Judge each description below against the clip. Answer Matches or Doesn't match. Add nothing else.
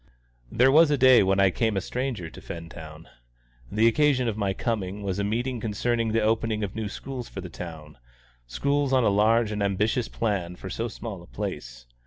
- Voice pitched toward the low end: Matches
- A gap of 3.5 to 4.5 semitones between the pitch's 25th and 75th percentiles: Matches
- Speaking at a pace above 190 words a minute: Matches